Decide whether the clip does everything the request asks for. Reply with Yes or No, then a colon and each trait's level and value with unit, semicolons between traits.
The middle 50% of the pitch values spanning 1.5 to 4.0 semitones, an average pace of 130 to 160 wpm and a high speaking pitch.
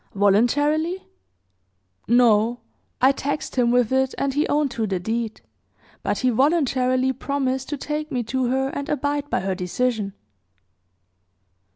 Yes: average, 3.4 semitones; average, 140 wpm; very high, 255 Hz